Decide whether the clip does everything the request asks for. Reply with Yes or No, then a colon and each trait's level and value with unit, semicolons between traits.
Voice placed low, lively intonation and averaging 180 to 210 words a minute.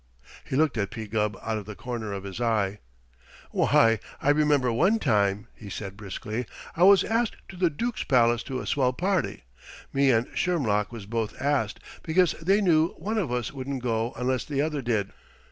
Yes: low, 125 Hz; wide, 6.1 semitones; average, 190 wpm